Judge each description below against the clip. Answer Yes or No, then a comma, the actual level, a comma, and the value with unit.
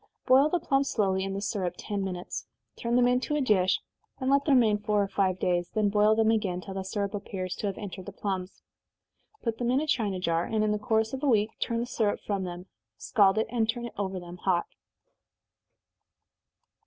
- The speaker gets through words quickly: Yes, fast, 215 wpm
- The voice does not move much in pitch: No, average, 3.7 semitones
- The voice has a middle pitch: No, high, 210 Hz